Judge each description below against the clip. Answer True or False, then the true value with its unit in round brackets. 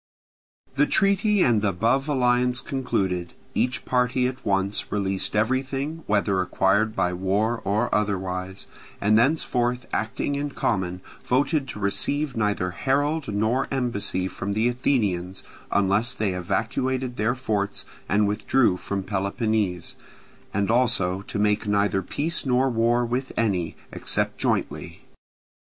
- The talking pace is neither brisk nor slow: False (125 wpm)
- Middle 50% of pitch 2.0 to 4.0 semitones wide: False (4.6 semitones)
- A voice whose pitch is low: True (110 Hz)